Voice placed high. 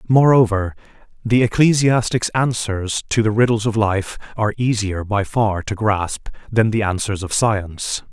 No: low, 110 Hz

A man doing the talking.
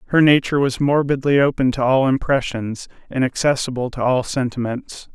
Yes: male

